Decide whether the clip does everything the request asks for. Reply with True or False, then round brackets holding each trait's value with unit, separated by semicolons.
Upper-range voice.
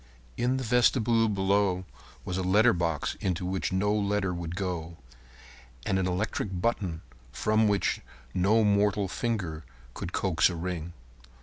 False (95 Hz)